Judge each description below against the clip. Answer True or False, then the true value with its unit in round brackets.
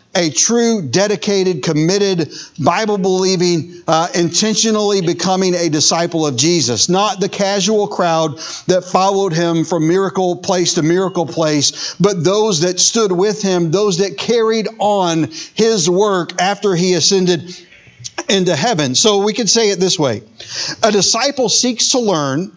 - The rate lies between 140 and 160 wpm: True (145 wpm)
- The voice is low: False (185 Hz)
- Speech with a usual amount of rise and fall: True (3.3 semitones)